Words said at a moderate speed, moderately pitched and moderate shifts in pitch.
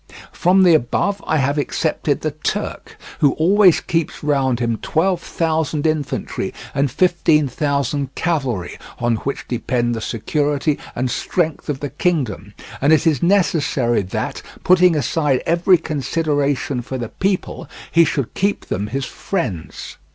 Yes: average, 145 wpm; medium, 145 Hz; average, 4.5 semitones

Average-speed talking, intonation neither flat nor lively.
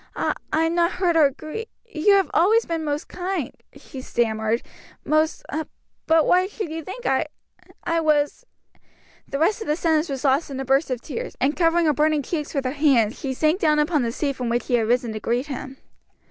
No: fast, 215 wpm; average, 3.9 semitones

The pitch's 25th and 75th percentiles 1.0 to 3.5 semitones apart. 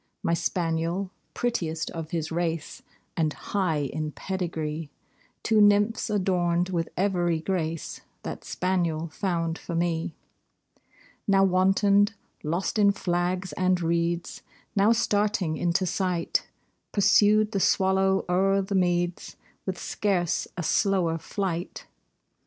Yes: average, 2.7 semitones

